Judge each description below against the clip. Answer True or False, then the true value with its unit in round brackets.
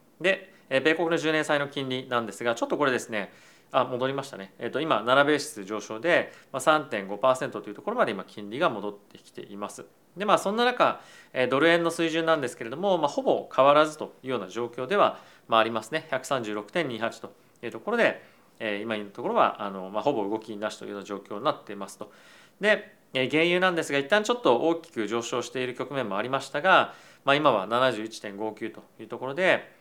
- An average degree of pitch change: False (6.6 semitones)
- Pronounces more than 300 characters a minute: True (380 characters per minute)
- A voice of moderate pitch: False (130 Hz)